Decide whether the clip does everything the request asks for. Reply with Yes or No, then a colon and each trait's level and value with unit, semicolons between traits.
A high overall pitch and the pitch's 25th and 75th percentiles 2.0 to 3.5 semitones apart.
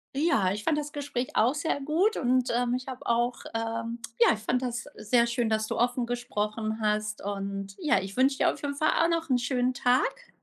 No: high, 245 Hz; average, 3.9 semitones